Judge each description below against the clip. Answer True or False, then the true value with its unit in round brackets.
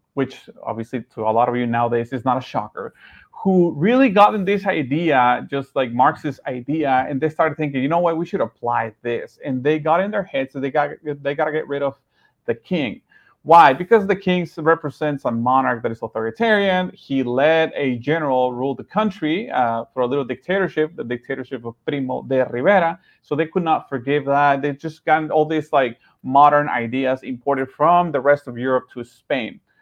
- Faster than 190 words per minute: True (200 wpm)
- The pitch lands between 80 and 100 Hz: False (140 Hz)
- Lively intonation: False (3.8 semitones)